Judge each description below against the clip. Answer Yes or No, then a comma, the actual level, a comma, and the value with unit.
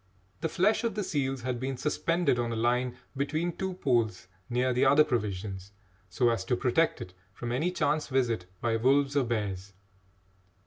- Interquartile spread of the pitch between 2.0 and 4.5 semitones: Yes, average, 4.2 semitones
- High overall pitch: No, low, 125 Hz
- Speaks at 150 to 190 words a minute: Yes, average, 175 wpm